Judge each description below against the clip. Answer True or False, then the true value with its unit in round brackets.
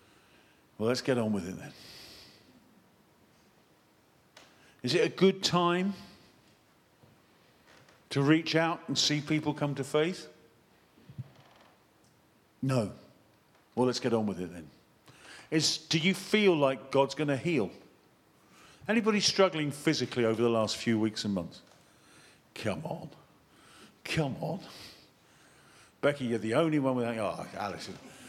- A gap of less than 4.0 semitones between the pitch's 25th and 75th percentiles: False (5.5 semitones)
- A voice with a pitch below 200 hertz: True (140 Hz)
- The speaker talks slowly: True (130 wpm)